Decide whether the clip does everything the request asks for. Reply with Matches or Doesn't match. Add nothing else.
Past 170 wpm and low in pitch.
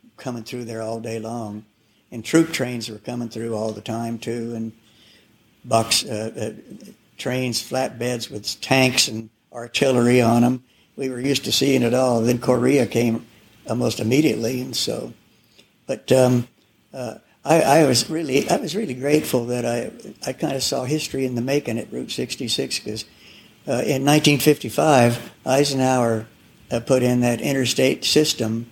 Doesn't match